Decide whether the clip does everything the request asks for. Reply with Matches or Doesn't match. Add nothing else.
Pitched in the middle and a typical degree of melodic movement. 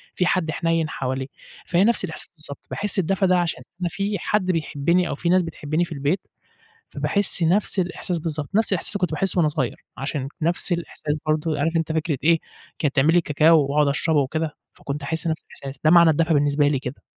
Matches